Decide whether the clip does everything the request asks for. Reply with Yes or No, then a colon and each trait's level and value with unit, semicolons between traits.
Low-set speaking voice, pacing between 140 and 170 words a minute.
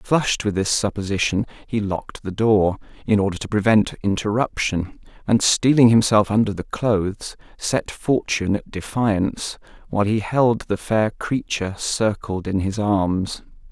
Yes: low, 105 Hz; average, 145 wpm